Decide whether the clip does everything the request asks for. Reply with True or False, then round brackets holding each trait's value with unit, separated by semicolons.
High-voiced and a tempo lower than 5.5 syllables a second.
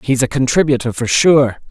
False (130 Hz; 5.2 syllables/s)